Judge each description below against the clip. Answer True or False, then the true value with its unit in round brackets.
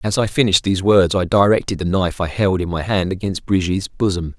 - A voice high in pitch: False (95 Hz)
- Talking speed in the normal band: False (235 wpm)